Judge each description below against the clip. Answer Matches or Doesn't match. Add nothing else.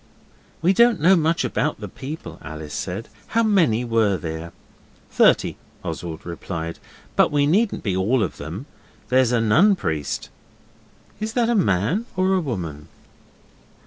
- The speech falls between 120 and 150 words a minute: Matches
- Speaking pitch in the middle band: Doesn't match